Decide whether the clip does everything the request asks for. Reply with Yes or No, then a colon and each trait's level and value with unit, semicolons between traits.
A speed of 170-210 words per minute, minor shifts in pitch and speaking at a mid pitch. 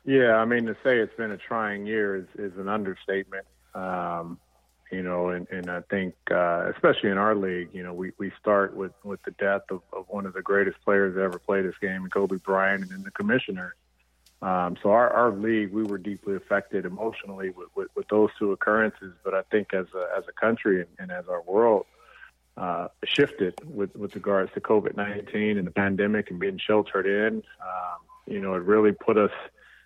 No: fast, 205 wpm; narrow, 2.3 semitones; low, 100 Hz